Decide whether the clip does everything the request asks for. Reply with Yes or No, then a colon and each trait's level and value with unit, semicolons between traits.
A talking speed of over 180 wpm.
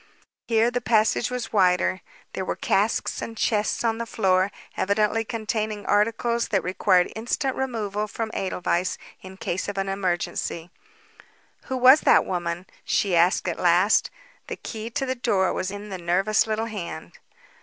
No: average, 155 wpm